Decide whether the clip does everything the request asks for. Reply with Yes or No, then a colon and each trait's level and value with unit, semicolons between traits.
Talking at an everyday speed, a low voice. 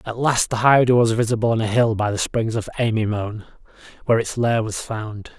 No: fast, 210 wpm; low, 115 Hz